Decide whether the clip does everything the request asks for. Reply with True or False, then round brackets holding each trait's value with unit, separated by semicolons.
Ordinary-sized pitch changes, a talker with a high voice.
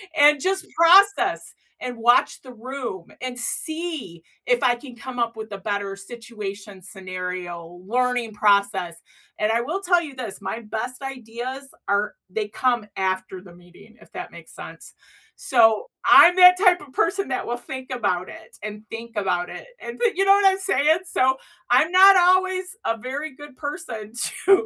False (7.3 semitones; 245 Hz)